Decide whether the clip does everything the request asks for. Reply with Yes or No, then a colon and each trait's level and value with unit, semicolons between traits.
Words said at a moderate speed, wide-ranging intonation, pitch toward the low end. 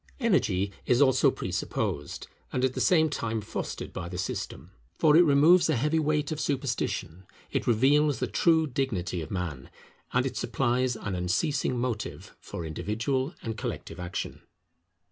Yes: average, 155 wpm; wide, 7.3 semitones; low, 125 Hz